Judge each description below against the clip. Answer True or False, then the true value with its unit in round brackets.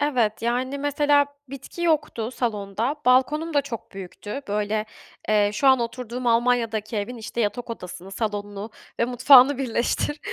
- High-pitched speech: True (240 Hz)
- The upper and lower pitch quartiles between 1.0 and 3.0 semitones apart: False (4.2 semitones)